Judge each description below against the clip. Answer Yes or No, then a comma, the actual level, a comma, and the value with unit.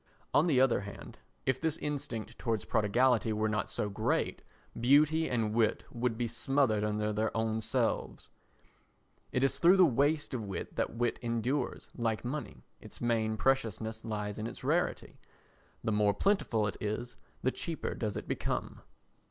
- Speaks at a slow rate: No, average, 160 wpm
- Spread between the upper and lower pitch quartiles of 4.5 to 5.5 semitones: No, average, 3.7 semitones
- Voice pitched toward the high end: No, low, 115 Hz